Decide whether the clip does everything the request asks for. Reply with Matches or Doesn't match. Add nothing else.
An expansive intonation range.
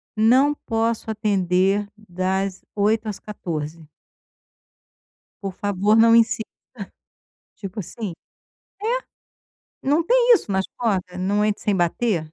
Doesn't match